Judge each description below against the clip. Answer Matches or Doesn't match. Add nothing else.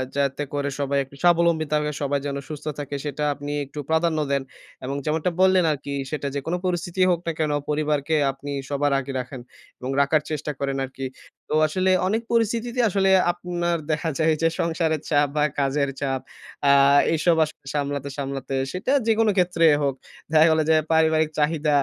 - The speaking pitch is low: Doesn't match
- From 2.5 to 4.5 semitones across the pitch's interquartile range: Matches